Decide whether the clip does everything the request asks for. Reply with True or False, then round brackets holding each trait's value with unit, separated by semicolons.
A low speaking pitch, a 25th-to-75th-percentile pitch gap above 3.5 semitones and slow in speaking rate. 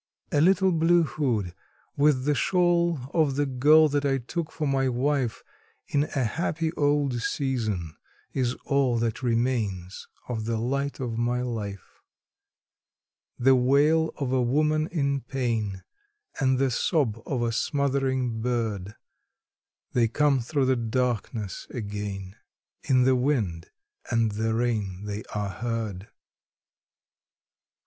True (125 Hz; 4.1 semitones; 130 wpm)